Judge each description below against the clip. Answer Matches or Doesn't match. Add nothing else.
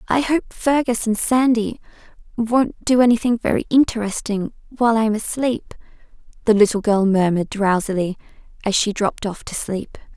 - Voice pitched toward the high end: Matches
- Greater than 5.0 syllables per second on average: Matches